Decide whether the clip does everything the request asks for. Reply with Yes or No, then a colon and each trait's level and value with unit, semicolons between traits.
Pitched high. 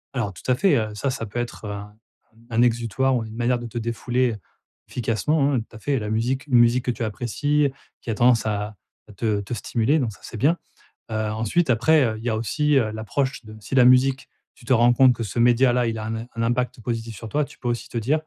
No: low, 120 Hz